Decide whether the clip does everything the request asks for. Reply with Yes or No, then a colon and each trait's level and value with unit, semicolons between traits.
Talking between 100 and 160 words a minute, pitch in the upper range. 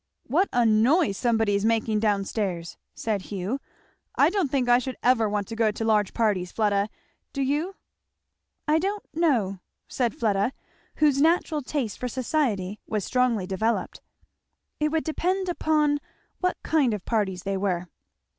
Yes: average, 155 wpm; high, 230 Hz